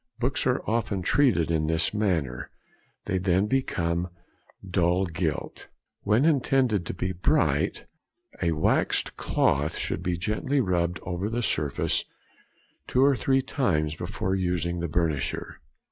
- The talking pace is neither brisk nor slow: No, slow, 130 wpm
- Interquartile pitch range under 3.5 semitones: No, average, 5.2 semitones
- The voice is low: Yes, very low, 90 Hz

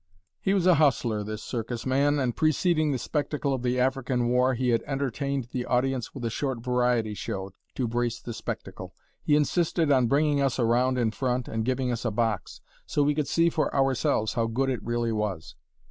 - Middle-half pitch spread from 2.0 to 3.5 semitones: Yes, average, 3.0 semitones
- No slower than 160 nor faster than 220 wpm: Yes, average, 200 wpm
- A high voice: No, low, 125 Hz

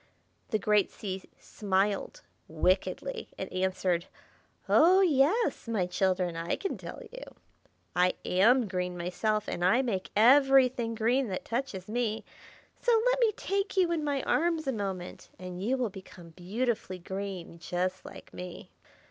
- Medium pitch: No, high, 210 Hz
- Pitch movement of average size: No, wide, 6.5 semitones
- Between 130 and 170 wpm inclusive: Yes, average, 145 wpm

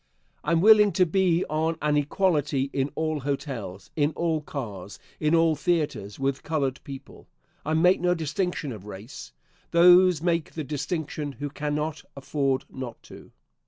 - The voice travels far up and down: No, average, 3.3 semitones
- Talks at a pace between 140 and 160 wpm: Yes, average, 155 wpm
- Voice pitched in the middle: Yes, medium, 150 Hz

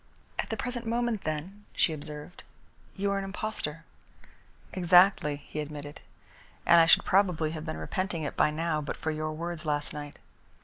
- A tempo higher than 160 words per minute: Yes, average, 170 wpm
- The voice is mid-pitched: Yes, medium, 165 Hz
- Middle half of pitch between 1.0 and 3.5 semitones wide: No, average, 4.3 semitones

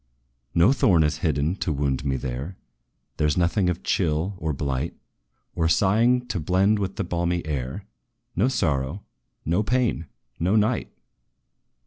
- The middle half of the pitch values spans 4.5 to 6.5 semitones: Yes, average, 4.9 semitones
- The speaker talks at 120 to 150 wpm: Yes, average, 145 wpm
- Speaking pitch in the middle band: No, very low, 85 Hz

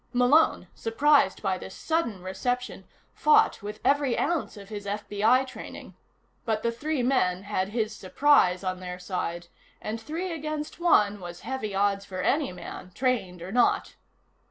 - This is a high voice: Yes, high, 215 Hz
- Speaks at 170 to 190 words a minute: No, average, 155 wpm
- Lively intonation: Yes, wide, 6.1 semitones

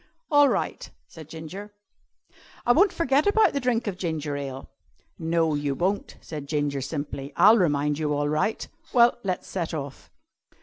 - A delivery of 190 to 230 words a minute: No, average, 160 wpm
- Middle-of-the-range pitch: Yes, medium, 160 Hz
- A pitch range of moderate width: No, wide, 7.0 semitones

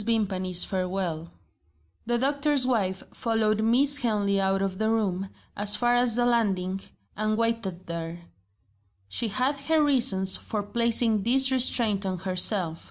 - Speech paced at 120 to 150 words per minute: Yes, average, 140 wpm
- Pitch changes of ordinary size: Yes, average, 4.1 semitones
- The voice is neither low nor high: No, high, 215 Hz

